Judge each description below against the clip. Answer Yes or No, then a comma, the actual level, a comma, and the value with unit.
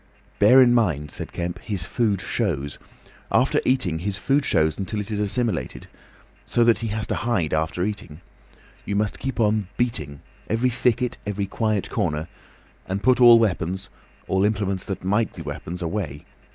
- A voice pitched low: Yes, low, 100 Hz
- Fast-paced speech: No, average, 165 wpm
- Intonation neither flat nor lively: Yes, average, 4.7 semitones